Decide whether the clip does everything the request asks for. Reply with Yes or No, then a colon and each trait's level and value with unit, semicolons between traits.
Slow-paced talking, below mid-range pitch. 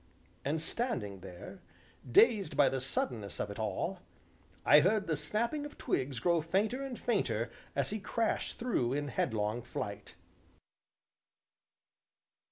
No: slow, 130 wpm; medium, 145 Hz